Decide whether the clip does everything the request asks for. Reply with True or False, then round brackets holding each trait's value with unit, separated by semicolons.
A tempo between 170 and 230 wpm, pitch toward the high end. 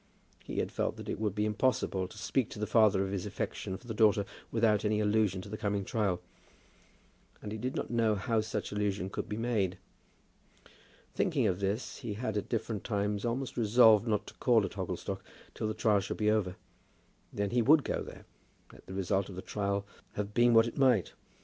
False (205 wpm; 105 Hz)